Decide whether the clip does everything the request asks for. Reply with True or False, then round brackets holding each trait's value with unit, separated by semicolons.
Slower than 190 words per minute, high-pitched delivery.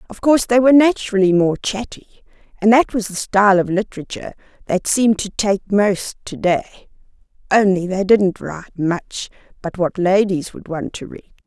True (175 wpm; 200 Hz)